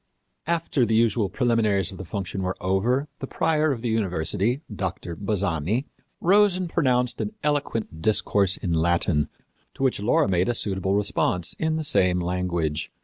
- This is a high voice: No, low, 100 Hz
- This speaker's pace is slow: No, average, 160 wpm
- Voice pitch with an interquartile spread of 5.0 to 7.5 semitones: Yes, wide, 5.6 semitones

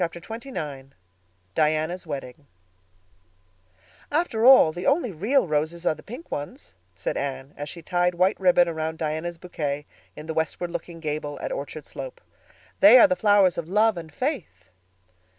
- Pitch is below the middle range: No, medium, 170 Hz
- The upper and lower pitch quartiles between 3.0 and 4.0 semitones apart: No, average, 5.2 semitones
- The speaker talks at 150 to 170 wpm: Yes, average, 160 wpm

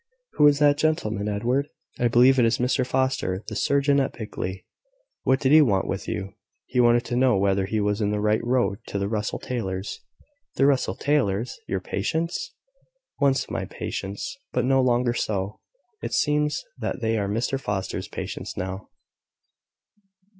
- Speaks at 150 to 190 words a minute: Yes, average, 165 wpm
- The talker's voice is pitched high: No, low, 120 Hz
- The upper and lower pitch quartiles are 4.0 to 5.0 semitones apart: Yes, average, 4.7 semitones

